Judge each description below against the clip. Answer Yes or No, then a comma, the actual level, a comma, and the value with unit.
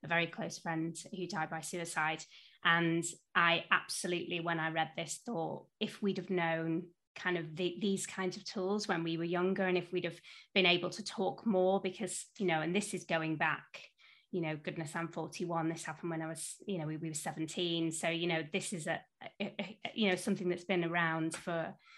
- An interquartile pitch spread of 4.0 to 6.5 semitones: No, narrow, 2.4 semitones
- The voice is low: No, medium, 175 Hz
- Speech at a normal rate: No, fast, 220 wpm